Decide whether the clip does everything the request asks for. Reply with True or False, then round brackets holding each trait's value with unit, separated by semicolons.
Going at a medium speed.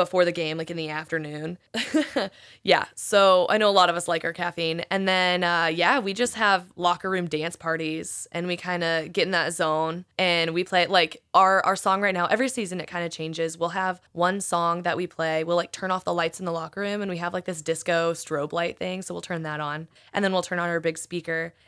False (250 wpm)